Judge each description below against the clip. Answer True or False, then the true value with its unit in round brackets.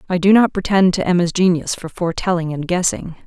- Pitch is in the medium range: True (180 Hz)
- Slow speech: False (200 wpm)